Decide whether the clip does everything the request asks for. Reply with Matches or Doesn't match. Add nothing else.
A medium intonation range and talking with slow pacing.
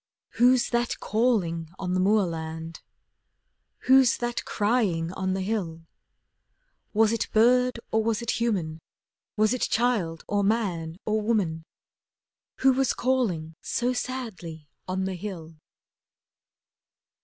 Doesn't match